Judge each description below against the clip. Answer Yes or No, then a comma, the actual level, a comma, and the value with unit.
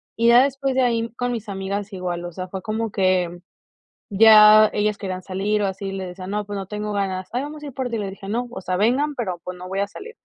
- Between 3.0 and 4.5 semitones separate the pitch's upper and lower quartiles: Yes, average, 3.5 semitones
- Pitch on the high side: Yes, high, 205 Hz